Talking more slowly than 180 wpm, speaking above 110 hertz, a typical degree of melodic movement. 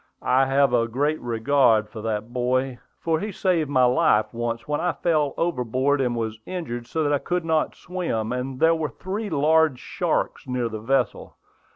No: average, 185 wpm; low, 135 Hz; average, 5.0 semitones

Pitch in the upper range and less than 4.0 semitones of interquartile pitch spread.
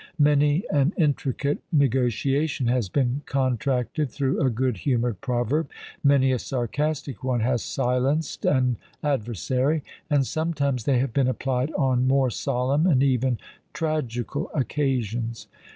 No: low, 130 Hz; narrow, 2.5 semitones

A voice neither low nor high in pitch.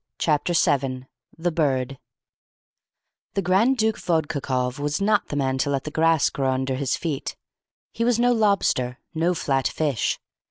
Yes: medium, 150 Hz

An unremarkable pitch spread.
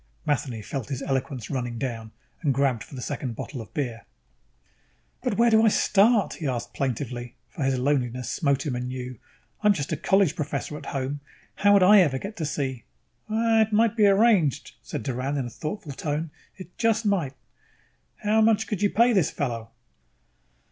No: wide, 8.0 semitones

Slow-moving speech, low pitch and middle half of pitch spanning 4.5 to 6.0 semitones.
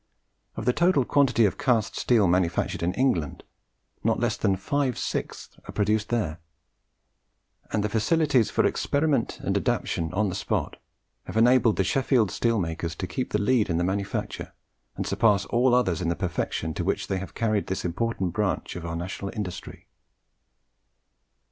No: average, 165 wpm; low, 105 Hz; average, 5.1 semitones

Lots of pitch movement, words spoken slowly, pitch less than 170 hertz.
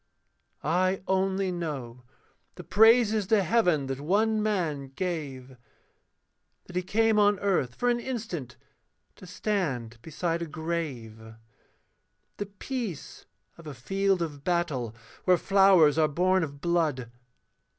No: wide, 5.7 semitones; slow, 125 wpm; medium, 175 Hz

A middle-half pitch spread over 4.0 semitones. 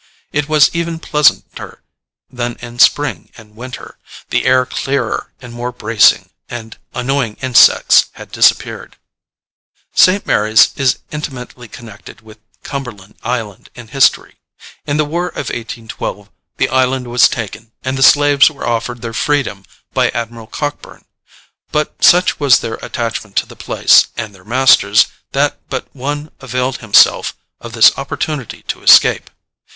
No: average, 3.7 semitones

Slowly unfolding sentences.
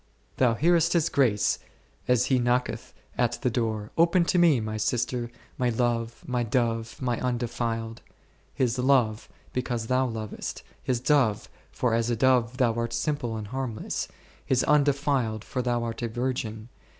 No: average, 160 wpm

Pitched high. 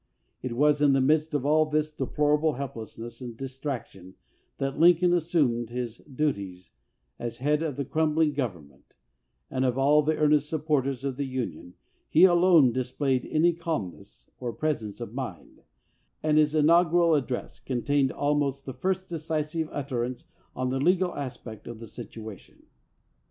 No: medium, 140 Hz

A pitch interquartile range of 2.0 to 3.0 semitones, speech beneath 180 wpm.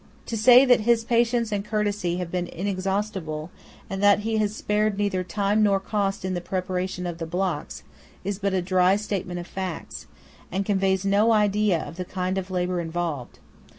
No: narrow, 2.5 semitones; average, 185 wpm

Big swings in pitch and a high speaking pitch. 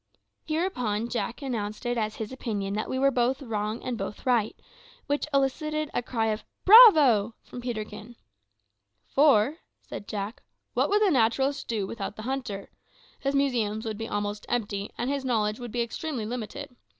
No: average, 4.2 semitones; high, 235 Hz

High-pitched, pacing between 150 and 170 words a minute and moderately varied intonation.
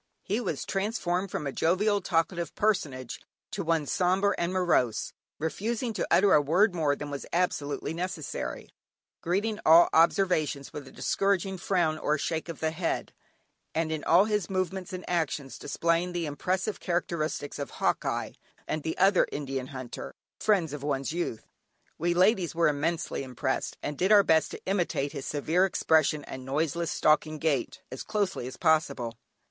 No: medium, 165 Hz; average, 160 wpm; average, 4.1 semitones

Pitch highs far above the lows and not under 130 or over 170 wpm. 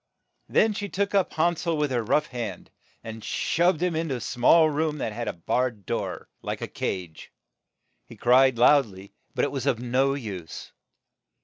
No: wide, 5.8 semitones; average, 190 wpm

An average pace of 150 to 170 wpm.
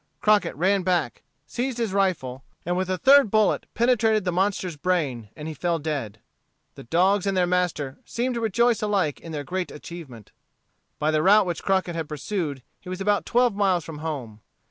No: average, 190 wpm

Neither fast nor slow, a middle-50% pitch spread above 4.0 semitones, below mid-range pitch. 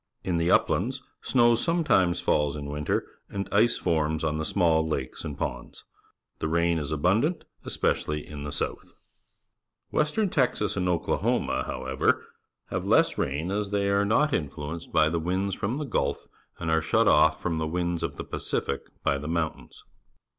Yes: average, 165 wpm; average, 4.6 semitones; very low, 85 Hz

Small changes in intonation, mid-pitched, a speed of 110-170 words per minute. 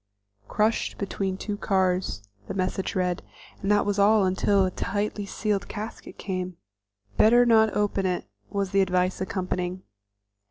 No: narrow, 2.1 semitones; high, 195 Hz; average, 145 wpm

